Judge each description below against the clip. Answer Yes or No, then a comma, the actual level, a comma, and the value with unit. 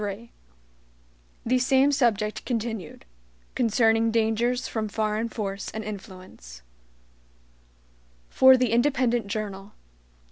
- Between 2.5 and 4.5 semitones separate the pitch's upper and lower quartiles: Yes, average, 2.8 semitones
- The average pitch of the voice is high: Yes, high, 225 Hz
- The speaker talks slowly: Yes, slow, 95 wpm